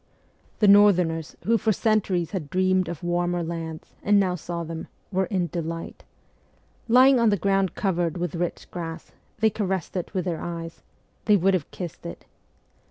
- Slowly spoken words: No, average, 165 wpm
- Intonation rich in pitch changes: No, average, 2.9 semitones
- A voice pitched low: No, medium, 180 Hz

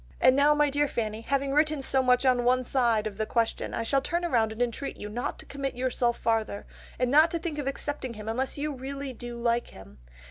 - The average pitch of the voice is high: Yes, very high, 255 Hz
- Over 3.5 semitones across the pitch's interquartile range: No, average, 3.2 semitones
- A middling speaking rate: No, fast, 235 wpm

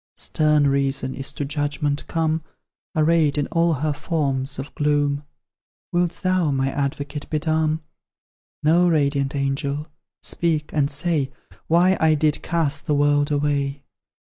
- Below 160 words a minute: Yes, slow, 135 wpm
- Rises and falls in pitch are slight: Yes, narrow, 2.1 semitones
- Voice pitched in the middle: Yes, medium, 150 Hz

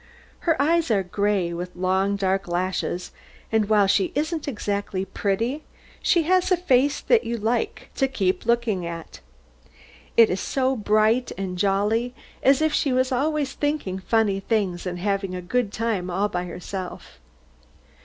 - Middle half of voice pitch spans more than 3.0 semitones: Yes, wide, 5.5 semitones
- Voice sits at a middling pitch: No, high, 210 Hz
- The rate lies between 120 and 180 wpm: Yes, average, 155 wpm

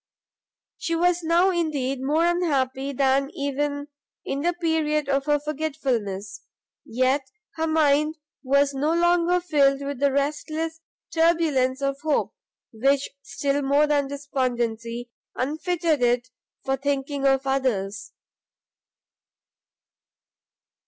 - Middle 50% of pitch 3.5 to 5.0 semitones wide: No, average, 2.9 semitones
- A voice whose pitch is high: Yes, very high, 280 Hz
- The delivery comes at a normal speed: No, slow, 110 wpm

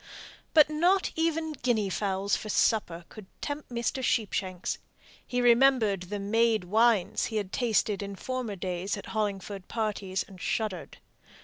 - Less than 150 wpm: Yes, average, 140 wpm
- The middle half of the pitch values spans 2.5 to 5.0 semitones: Yes, average, 3.9 semitones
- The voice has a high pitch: Yes, high, 215 Hz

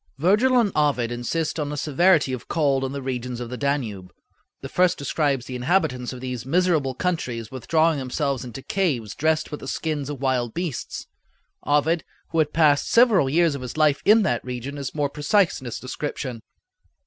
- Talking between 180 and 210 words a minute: Yes, average, 185 wpm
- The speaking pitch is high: No, medium, 140 Hz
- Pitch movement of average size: Yes, average, 4.3 semitones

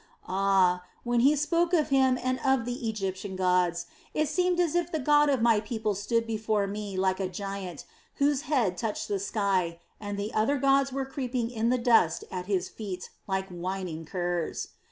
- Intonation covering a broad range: Yes, wide, 5.8 semitones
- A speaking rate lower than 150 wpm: No, average, 185 wpm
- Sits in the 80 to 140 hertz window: No, high, 215 Hz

